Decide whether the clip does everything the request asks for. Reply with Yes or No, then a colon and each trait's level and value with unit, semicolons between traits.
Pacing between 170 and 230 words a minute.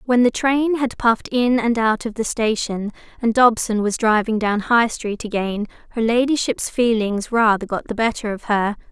Yes: average, 190 wpm